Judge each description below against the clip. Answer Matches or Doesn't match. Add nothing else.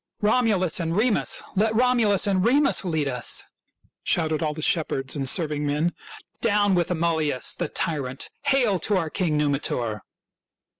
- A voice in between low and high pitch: Matches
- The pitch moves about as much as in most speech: Doesn't match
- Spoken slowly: Doesn't match